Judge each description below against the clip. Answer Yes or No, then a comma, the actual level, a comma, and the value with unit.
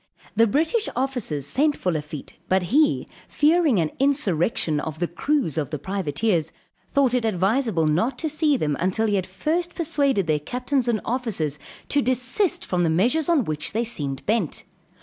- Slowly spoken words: No, average, 170 wpm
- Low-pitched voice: No, high, 225 Hz